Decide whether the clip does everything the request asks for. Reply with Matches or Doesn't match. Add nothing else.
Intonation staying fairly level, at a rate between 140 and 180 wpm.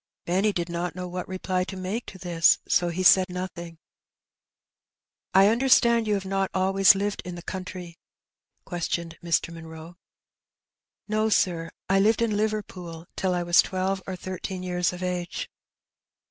Matches